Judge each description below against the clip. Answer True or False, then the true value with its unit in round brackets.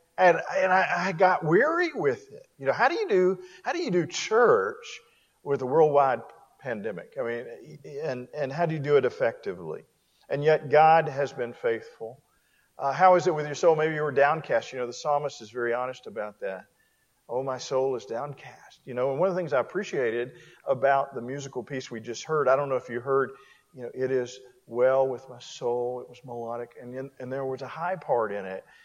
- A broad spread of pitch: True (6.2 semitones)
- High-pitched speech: False (140 Hz)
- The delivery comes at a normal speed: False (220 wpm)